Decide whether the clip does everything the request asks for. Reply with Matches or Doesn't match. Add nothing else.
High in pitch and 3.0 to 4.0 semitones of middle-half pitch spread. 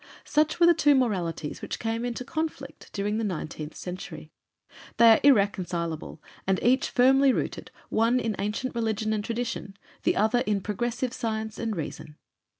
Matches